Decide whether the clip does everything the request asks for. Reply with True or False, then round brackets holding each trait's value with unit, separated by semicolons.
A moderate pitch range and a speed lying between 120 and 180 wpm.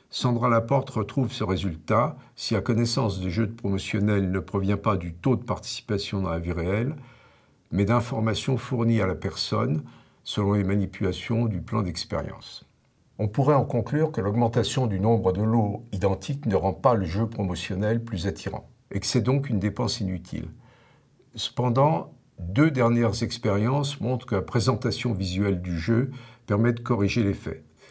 True (3.8 semitones; 165 wpm)